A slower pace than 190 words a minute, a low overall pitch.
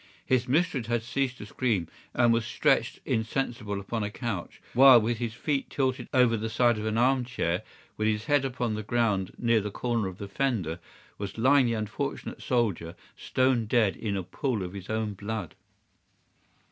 Yes: average, 180 wpm; low, 115 Hz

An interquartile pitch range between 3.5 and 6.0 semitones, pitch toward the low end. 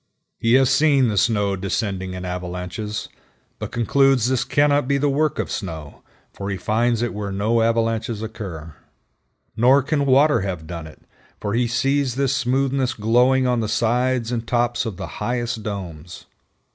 Yes: average, 4.5 semitones; low, 115 Hz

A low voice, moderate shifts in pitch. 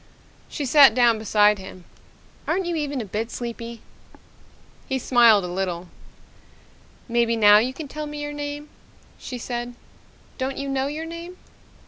No: high, 245 Hz; average, 4.9 semitones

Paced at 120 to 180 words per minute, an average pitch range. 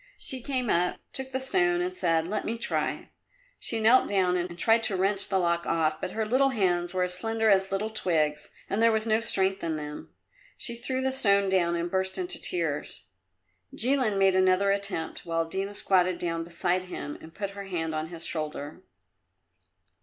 No: average, 190 wpm; average, 4.6 semitones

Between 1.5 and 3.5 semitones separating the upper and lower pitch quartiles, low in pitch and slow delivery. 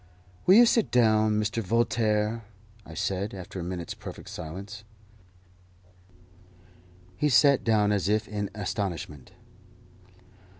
Yes: average, 3.0 semitones; low, 105 Hz; slow, 115 wpm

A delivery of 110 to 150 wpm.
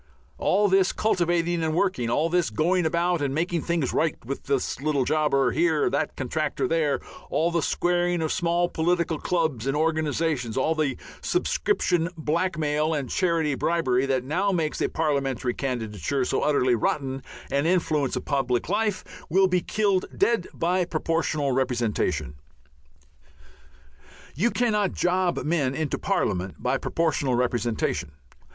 Yes: average, 140 wpm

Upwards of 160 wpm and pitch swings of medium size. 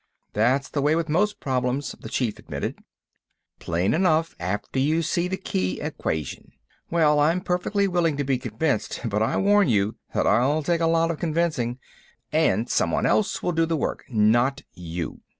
No: average, 170 wpm; wide, 6.3 semitones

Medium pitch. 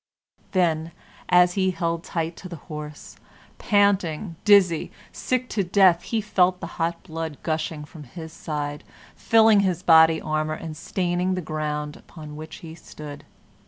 Yes: medium, 165 Hz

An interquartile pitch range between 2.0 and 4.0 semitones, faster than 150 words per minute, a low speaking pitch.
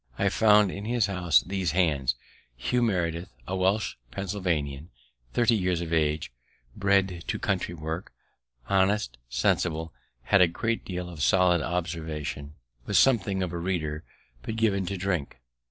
No: average, 3.5 semitones; average, 145 wpm; very low, 90 Hz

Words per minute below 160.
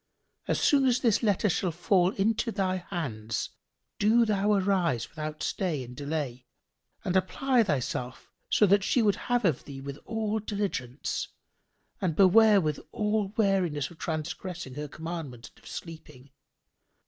Yes: average, 150 wpm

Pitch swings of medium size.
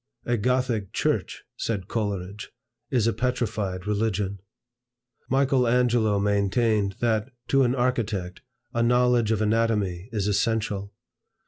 Yes: average, 3.2 semitones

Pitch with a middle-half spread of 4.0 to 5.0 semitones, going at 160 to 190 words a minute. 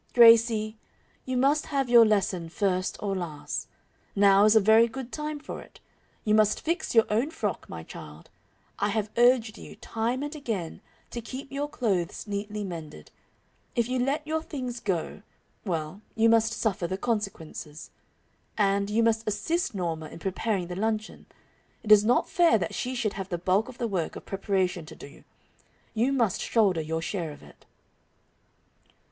Yes: average, 4.3 semitones; average, 170 wpm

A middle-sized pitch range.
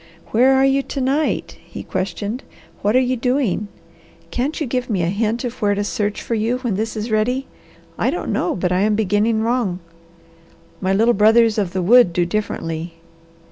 Yes: average, 3.7 semitones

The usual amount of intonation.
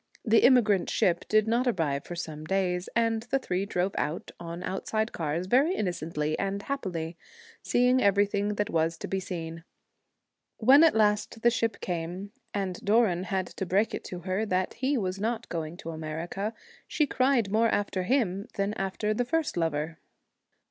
Yes: average, 4.5 semitones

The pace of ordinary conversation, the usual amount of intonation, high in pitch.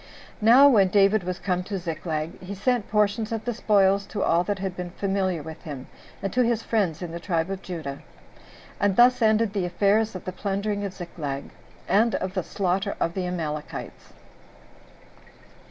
Yes: average, 180 wpm; average, 3.1 semitones; high, 195 Hz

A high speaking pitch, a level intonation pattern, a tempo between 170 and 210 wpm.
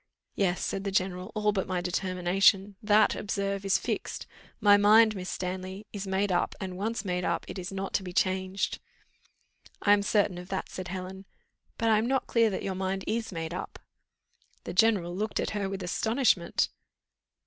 Yes: high, 195 Hz; narrow, 2.0 semitones; average, 185 wpm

